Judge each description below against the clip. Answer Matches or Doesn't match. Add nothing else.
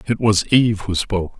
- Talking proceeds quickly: Matches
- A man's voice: Matches